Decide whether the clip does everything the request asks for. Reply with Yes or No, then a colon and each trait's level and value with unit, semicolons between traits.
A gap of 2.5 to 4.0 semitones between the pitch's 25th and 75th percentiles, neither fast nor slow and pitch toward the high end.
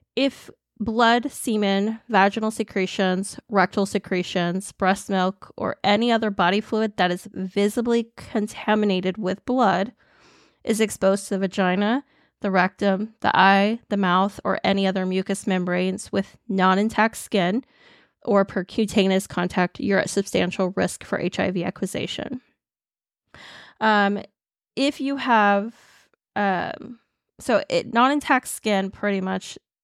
No: average, 3.1 semitones; slow, 125 wpm; high, 200 Hz